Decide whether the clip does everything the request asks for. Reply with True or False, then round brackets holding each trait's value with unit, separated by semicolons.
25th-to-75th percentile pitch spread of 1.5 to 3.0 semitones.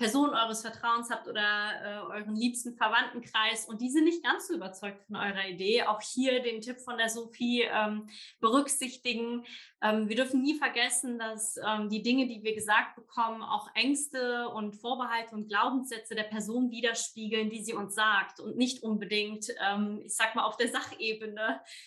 True (2.4 semitones)